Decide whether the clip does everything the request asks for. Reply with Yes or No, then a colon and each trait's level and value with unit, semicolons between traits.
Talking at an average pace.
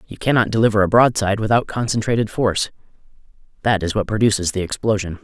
Yes: average, 150 wpm